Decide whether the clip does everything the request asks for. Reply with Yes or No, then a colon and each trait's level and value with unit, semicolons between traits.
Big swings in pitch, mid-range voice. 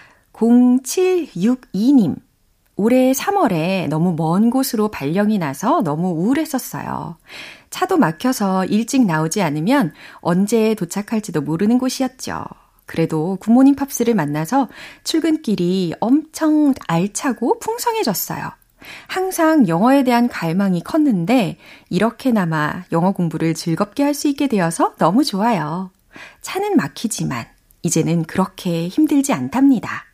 No: wide, 7.5 semitones; high, 225 Hz